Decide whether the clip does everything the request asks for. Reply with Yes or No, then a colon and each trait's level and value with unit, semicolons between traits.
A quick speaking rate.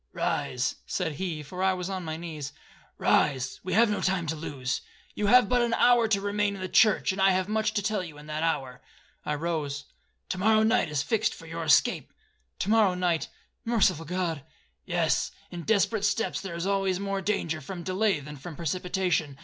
No: average, 190 wpm